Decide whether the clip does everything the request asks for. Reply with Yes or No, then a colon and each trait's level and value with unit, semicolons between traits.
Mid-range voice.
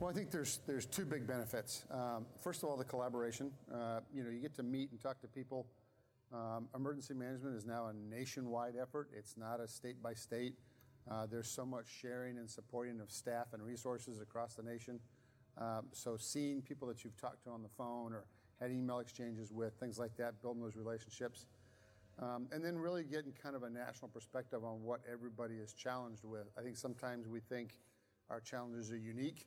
No: low, 120 Hz